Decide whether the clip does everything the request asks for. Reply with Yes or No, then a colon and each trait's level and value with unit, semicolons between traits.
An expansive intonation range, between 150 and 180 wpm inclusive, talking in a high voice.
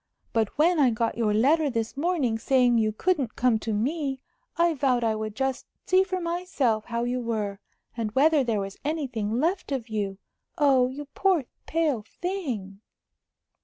Yes: wide, 5.7 semitones; average, 165 wpm; very high, 255 Hz